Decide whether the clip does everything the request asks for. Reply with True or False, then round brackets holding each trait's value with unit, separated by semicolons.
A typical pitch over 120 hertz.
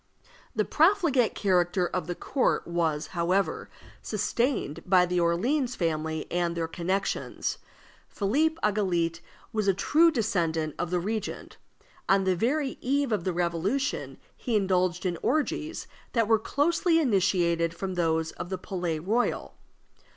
True (190 Hz)